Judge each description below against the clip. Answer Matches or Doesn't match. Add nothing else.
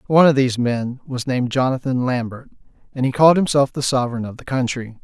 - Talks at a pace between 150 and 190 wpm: Doesn't match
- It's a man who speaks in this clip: Matches